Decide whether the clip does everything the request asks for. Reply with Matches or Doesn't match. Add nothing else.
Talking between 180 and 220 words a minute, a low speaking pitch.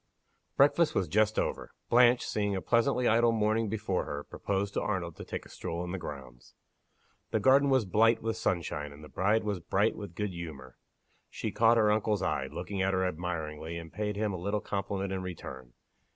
Matches